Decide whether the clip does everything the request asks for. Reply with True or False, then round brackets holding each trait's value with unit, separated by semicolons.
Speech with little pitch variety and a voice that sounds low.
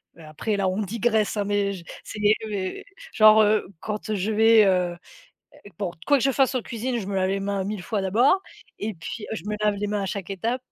False (2.1 semitones; 210 Hz)